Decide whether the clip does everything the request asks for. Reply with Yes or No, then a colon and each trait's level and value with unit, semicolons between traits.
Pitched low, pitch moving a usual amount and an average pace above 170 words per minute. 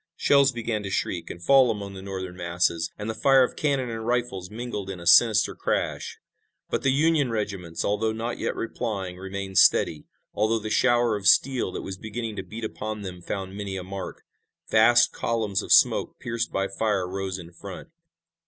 Yes: low, 105 Hz; average, 3.5 semitones; average, 190 wpm